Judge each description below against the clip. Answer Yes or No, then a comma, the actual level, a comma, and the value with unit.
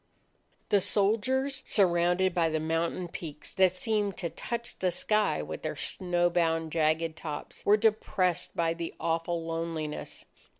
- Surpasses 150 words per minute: No, average, 140 wpm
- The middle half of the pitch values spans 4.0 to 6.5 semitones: No, average, 3.3 semitones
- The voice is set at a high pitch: No, medium, 175 Hz